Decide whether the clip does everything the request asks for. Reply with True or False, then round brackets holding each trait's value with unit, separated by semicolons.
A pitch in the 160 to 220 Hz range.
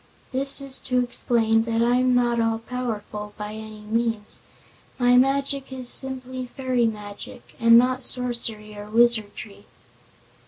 False (235 Hz)